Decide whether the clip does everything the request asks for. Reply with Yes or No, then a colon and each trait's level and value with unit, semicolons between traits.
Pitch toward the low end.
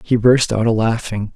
Yes: low, 115 Hz